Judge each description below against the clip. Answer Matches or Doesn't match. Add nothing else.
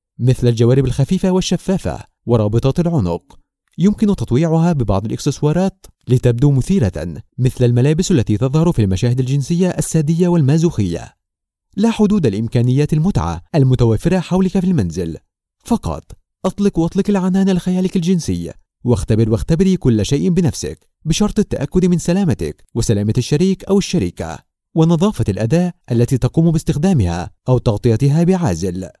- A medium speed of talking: Matches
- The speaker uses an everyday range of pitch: Doesn't match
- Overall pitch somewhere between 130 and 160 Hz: Matches